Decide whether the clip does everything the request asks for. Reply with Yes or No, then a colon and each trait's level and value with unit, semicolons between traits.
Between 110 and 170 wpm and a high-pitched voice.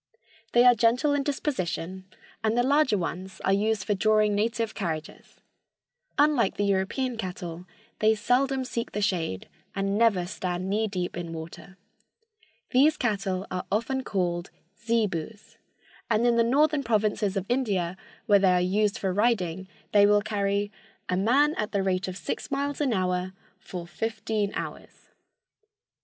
Yes: average, 150 wpm; high, 205 Hz